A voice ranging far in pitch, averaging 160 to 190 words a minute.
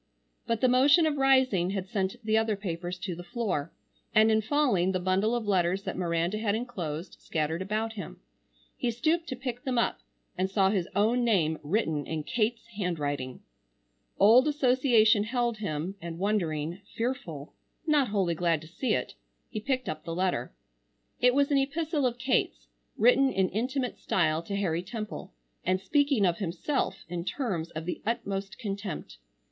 Yes: wide, 5.8 semitones; average, 170 wpm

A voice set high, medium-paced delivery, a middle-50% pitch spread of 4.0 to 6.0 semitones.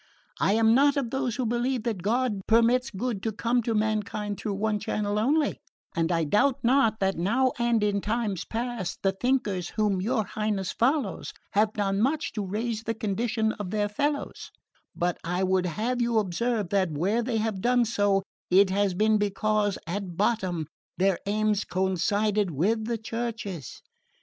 No: high, 215 Hz; average, 170 wpm; average, 3.2 semitones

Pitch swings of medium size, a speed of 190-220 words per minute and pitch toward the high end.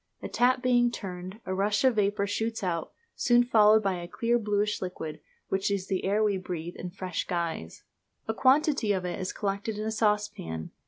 Yes: average, 3.3 semitones; average, 200 wpm; high, 205 Hz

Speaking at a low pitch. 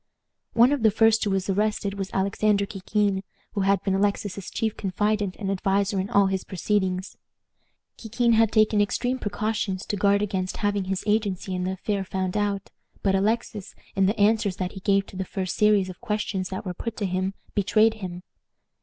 No: high, 200 Hz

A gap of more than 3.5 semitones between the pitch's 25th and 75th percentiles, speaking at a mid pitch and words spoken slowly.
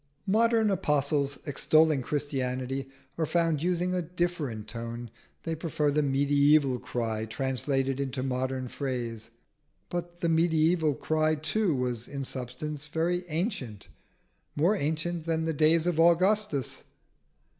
Yes: average, 4.1 semitones; medium, 150 Hz; slow, 125 wpm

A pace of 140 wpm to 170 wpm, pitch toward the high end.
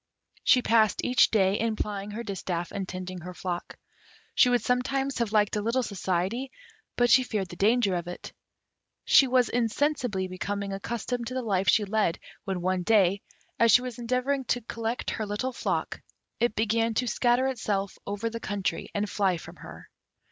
No: average, 180 wpm; high, 215 Hz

